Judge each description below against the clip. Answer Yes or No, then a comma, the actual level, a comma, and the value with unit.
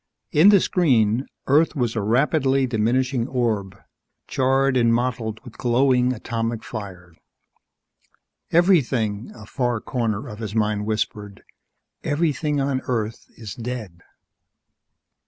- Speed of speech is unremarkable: No, slow, 115 wpm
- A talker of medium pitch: No, low, 120 Hz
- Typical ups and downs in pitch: Yes, average, 3.7 semitones